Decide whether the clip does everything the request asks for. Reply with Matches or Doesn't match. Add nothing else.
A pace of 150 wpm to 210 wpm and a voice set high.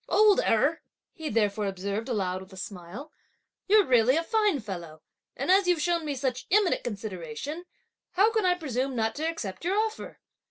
Matches